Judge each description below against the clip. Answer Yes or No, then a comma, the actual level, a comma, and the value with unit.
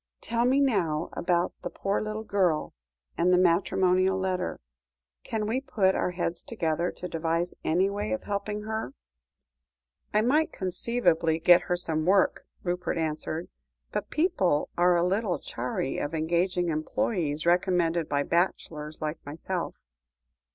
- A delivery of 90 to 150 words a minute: Yes, average, 140 wpm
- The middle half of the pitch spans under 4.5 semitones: Yes, average, 3.4 semitones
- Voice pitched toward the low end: No, medium, 180 Hz